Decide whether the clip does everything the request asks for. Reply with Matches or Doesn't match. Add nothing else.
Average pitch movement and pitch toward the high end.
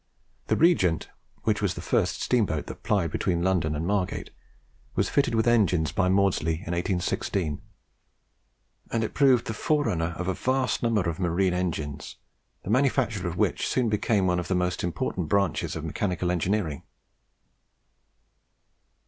Doesn't match